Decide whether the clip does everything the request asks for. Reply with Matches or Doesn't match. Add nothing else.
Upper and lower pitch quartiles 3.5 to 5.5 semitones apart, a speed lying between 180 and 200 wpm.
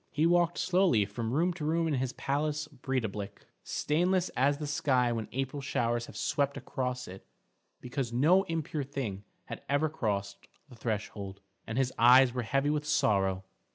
Doesn't match